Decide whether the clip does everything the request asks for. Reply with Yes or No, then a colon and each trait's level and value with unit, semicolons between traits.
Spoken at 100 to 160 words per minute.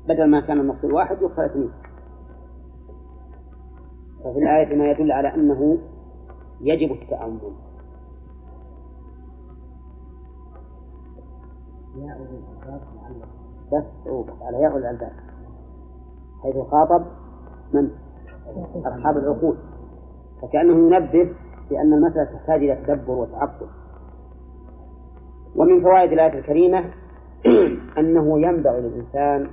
No: average, 80 wpm